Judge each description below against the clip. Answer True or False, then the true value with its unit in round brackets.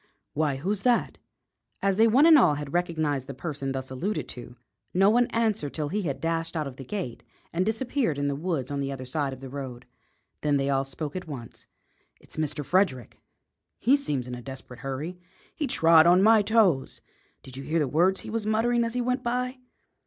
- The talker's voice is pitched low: False (160 Hz)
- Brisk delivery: True (210 wpm)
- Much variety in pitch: True (7.6 semitones)